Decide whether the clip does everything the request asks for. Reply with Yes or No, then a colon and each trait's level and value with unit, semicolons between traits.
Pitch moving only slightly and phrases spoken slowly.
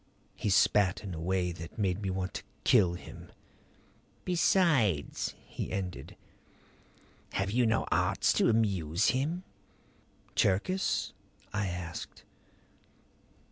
No: average, 4.1 semitones; slow, 110 wpm